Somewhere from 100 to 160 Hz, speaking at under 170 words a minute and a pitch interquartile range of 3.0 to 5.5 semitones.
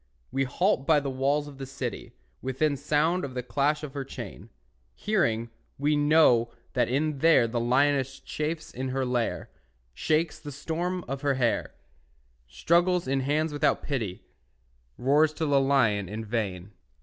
Yes: medium, 140 Hz; average, 160 wpm; average, 3.3 semitones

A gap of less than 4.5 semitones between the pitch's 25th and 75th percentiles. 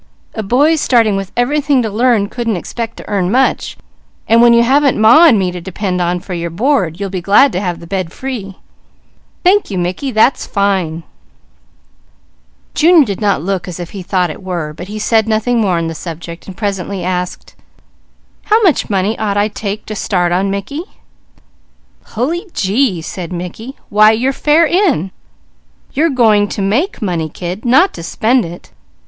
No: average, 5.3 semitones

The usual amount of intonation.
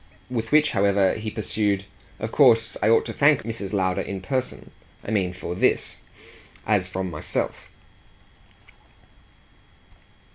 Yes: average, 3.1 semitones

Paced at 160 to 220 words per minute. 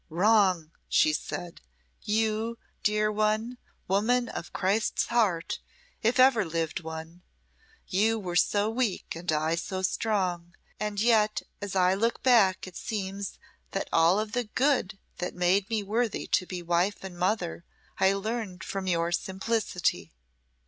No: average, 140 wpm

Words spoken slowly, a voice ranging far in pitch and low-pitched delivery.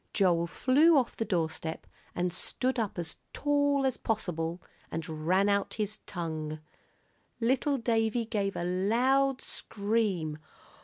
No: slow, 125 wpm; wide, 6.6 semitones; high, 205 Hz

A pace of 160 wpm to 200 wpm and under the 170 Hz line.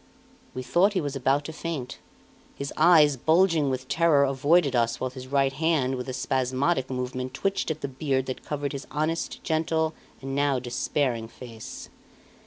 Yes: average, 170 wpm; medium, 140 Hz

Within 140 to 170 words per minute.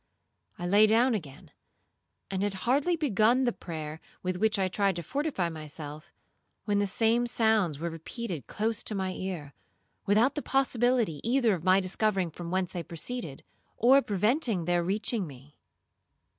Yes: average, 155 wpm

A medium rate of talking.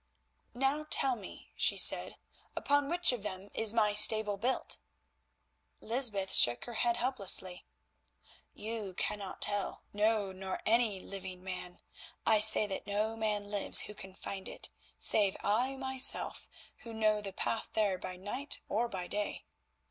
Yes: average, 150 wpm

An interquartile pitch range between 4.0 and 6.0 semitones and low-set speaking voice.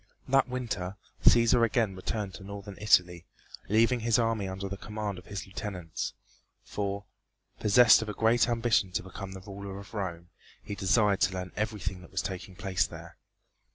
No: average, 2.9 semitones; low, 100 Hz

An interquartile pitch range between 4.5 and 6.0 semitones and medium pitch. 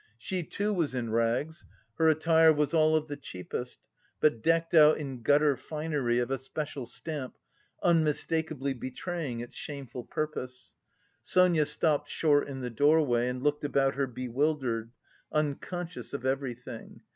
No: average, 3.8 semitones; medium, 145 Hz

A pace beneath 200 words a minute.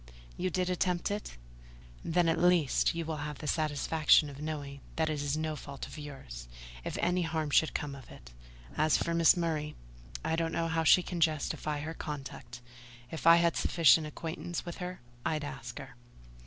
Yes: average, 185 wpm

